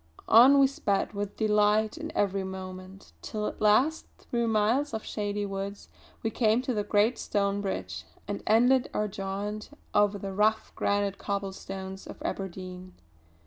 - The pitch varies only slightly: Yes, narrow, 2.0 semitones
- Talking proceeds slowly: No, average, 150 wpm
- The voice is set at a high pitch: Yes, high, 205 Hz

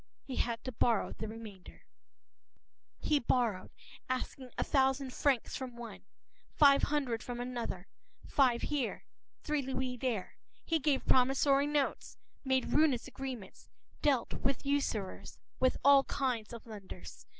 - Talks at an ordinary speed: No, slow, 130 wpm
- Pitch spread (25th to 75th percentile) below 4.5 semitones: Yes, average, 2.9 semitones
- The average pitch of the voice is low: No, very high, 255 Hz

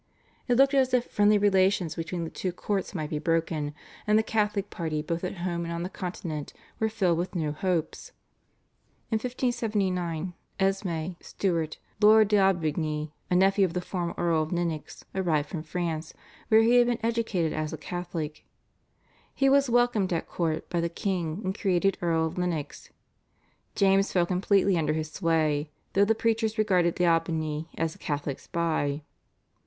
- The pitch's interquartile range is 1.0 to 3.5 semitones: No, average, 3.9 semitones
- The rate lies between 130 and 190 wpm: Yes, average, 165 wpm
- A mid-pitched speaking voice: Yes, medium, 175 Hz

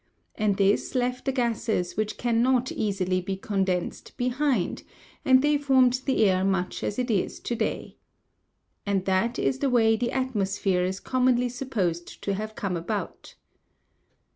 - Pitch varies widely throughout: No, average, 4.6 semitones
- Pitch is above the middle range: Yes, high, 220 Hz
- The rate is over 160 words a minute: No, average, 150 wpm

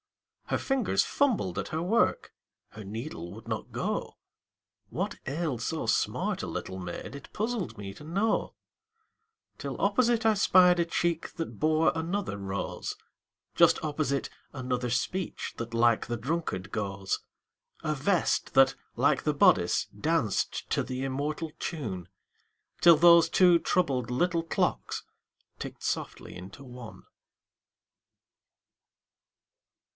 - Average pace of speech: No, slow, 125 wpm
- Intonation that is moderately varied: No, wide, 6.9 semitones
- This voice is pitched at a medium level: Yes, medium, 145 Hz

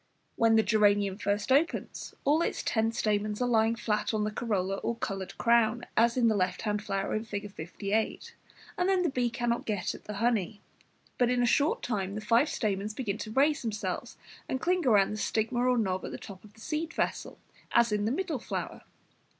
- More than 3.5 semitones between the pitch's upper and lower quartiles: No, average, 3.0 semitones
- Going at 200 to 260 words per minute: Yes, fast, 205 wpm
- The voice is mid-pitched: No, high, 220 Hz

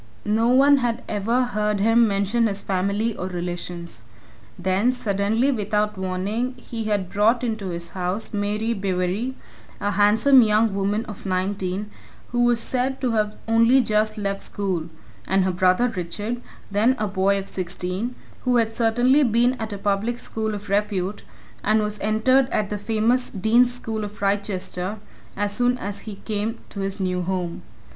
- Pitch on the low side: No, high, 210 Hz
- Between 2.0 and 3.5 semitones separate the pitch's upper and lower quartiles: Yes, average, 2.9 semitones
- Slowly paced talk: No, average, 165 wpm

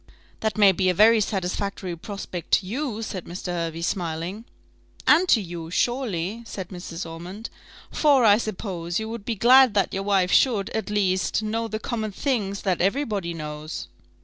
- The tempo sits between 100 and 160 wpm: No, average, 175 wpm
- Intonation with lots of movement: No, average, 4.0 semitones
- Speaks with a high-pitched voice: Yes, high, 200 Hz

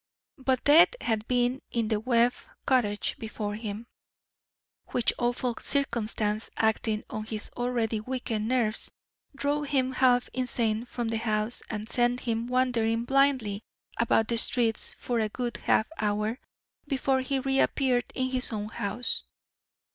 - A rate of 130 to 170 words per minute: Yes, average, 140 wpm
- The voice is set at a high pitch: Yes, high, 235 Hz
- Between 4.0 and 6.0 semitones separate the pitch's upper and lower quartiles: No, average, 2.7 semitones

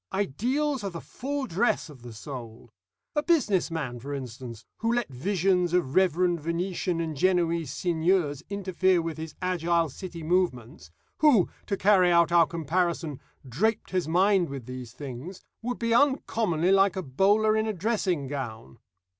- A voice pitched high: No, medium, 175 Hz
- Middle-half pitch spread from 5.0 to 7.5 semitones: Yes, average, 5.3 semitones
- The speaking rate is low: No, average, 155 wpm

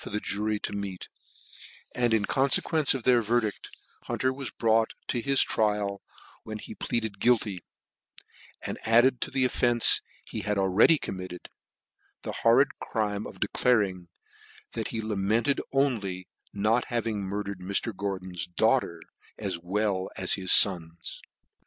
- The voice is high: No, low, 105 Hz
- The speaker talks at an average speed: Yes, average, 145 wpm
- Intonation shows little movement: No, average, 3.5 semitones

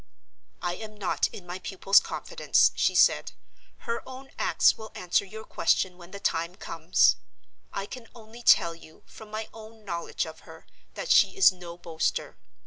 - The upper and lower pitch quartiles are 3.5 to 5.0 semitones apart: Yes, average, 3.9 semitones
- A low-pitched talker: No, high, 195 Hz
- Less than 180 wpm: Yes, average, 170 wpm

